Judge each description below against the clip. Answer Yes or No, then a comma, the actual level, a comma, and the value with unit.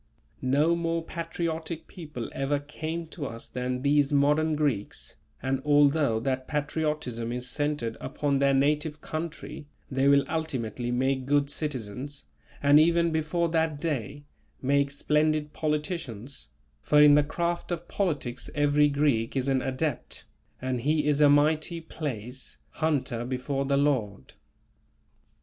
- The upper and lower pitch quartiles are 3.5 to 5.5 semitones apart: No, average, 3.0 semitones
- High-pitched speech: No, medium, 145 Hz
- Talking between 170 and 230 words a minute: No, slow, 135 wpm